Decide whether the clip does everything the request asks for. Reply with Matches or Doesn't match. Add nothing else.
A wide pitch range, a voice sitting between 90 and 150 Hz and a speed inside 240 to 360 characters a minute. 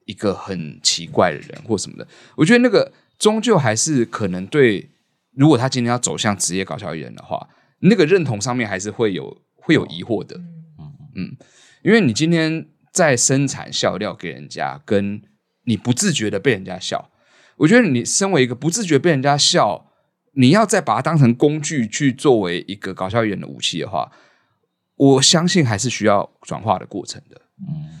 Matches